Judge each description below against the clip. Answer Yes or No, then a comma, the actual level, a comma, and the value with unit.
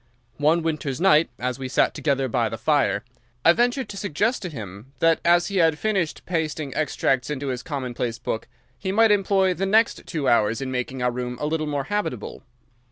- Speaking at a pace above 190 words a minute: Yes, average, 200 wpm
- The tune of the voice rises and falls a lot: Yes, wide, 6.3 semitones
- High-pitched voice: No, medium, 150 Hz